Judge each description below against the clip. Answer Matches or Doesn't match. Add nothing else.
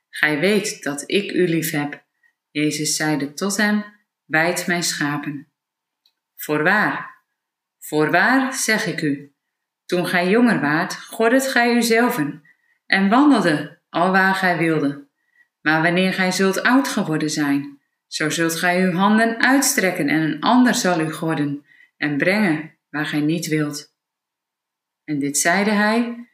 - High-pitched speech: Doesn't match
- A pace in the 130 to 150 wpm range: Matches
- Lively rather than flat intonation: Matches